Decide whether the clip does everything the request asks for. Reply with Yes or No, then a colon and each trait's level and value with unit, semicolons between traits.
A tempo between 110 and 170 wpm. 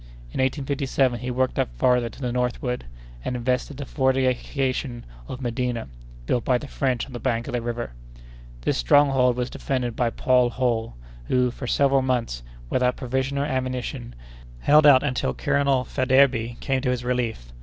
Yes: average, 165 wpm